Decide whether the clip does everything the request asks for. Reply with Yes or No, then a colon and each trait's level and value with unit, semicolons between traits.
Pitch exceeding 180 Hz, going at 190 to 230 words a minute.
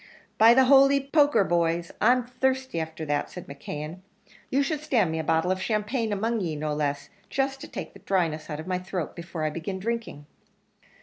Yes: high, 190 Hz; average, 195 wpm